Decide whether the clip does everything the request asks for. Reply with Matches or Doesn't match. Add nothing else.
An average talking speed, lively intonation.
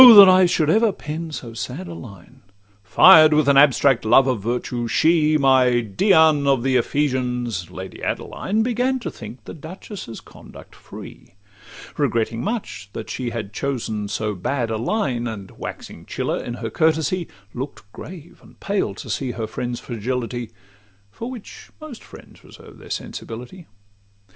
Matches